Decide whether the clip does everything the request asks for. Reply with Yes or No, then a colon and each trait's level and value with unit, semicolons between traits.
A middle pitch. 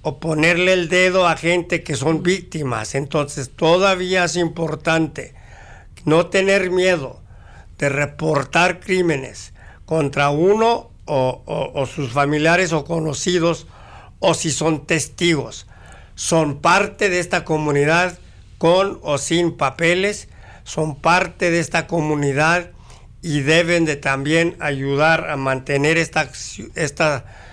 Yes: medium, 155 Hz